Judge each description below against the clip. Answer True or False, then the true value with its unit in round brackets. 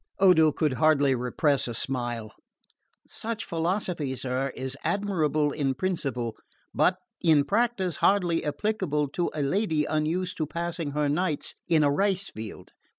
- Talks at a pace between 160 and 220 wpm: False (140 wpm)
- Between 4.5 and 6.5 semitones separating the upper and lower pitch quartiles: True (4.8 semitones)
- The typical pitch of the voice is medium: True (155 Hz)